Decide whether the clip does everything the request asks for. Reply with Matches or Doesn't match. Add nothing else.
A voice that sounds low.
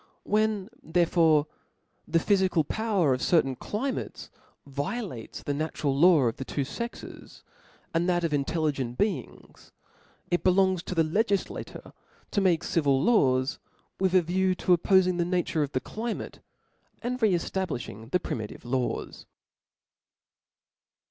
Doesn't match